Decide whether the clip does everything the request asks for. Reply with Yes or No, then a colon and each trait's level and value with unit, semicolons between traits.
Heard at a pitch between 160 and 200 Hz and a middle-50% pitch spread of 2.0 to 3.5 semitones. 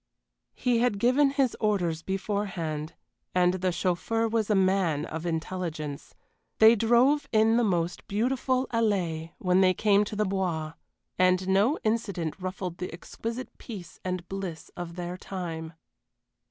No: high, 190 Hz; average, 4.3 semitones